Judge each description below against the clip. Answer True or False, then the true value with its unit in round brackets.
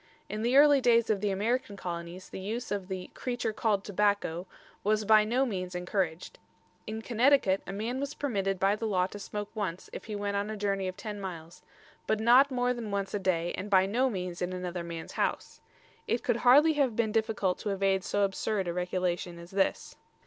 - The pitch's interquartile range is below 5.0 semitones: True (3.4 semitones)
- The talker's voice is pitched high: True (205 Hz)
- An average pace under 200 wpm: False (205 wpm)